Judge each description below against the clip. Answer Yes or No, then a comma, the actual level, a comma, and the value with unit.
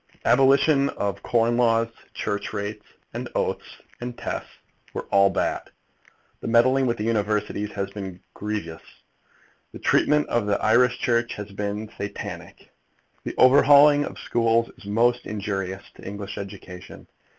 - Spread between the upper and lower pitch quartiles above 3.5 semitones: No, average, 3.1 semitones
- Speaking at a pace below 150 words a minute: Yes, average, 140 wpm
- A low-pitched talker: Yes, low, 110 Hz